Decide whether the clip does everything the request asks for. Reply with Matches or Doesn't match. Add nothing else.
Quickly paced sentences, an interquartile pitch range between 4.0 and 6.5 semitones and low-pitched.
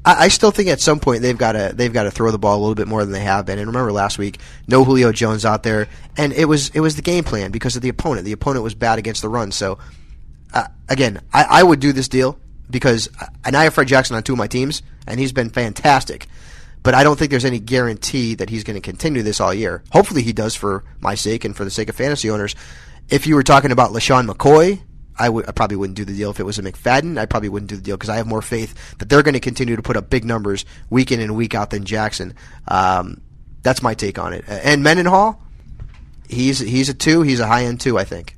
Matches